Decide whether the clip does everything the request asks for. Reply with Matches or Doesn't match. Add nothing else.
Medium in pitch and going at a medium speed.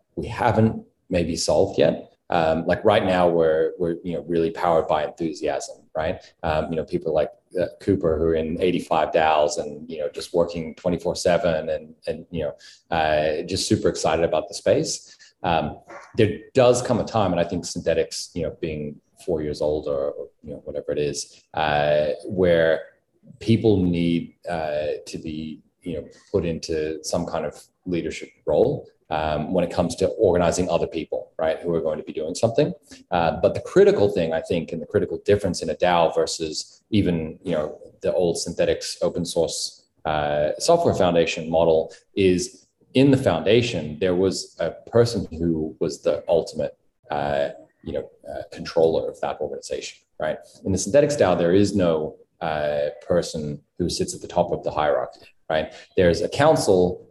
Doesn't match